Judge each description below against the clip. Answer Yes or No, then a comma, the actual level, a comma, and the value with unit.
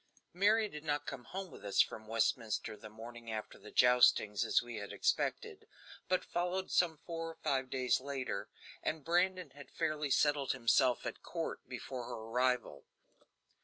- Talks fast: No, average, 165 wpm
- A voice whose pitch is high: No, low, 130 Hz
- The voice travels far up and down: Yes, wide, 5.7 semitones